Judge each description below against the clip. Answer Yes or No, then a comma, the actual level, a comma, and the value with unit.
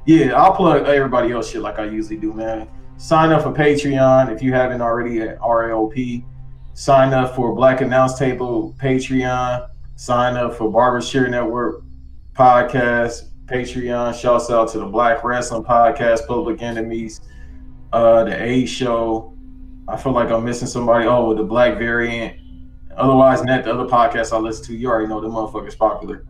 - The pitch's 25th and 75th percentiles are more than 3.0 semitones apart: No, narrow, 2.4 semitones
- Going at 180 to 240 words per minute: No, average, 170 wpm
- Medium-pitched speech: No, low, 120 Hz